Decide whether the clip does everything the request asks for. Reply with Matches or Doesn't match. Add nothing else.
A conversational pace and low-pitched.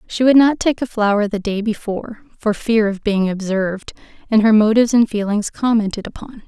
Doesn't match